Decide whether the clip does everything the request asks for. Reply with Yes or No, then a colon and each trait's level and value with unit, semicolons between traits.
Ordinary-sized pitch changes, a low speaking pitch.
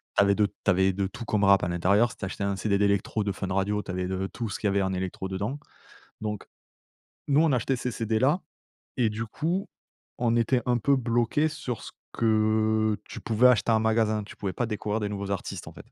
Yes: average, 3.0 semitones; low, 110 Hz